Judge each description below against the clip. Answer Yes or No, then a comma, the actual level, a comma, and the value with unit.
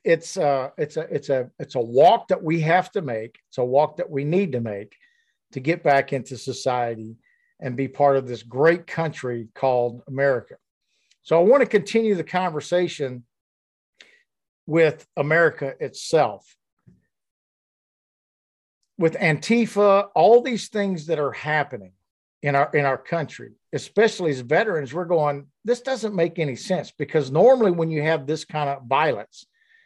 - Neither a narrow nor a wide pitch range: No, wide, 5.7 semitones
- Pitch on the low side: No, medium, 150 Hz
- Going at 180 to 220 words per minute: No, average, 155 wpm